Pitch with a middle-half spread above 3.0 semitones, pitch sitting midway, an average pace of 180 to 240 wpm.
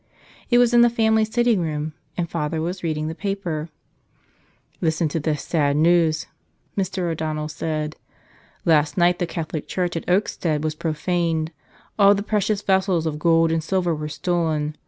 No: average, 3.4 semitones; medium, 165 Hz; average, 165 wpm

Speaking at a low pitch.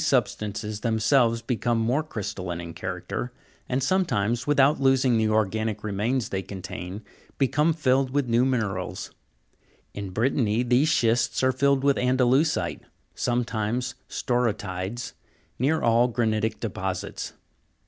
Yes: low, 120 Hz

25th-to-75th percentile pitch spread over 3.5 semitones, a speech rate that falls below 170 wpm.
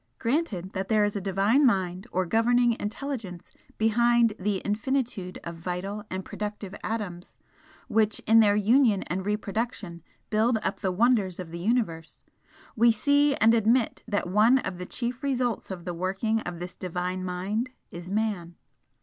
Yes: average, 4.0 semitones; average, 160 wpm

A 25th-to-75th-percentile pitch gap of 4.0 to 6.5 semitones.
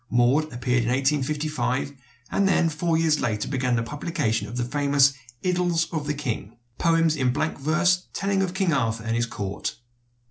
Yes: average, 5.2 semitones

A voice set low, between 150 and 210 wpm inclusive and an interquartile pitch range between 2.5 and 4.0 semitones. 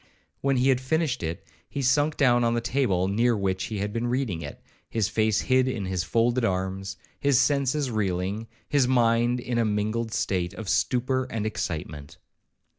No: low, 115 Hz; average, 180 wpm; average, 4.9 semitones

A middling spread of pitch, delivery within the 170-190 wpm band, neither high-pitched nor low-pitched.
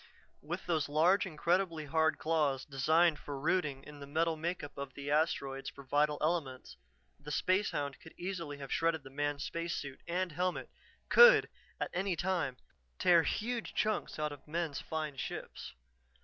No: average, 3.3 semitones; average, 160 wpm; medium, 155 Hz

